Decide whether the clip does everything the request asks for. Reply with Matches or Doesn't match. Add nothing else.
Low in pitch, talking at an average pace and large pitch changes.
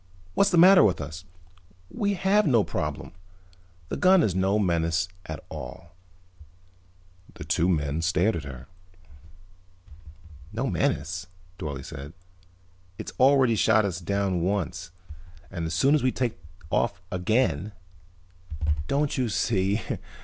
Doesn't match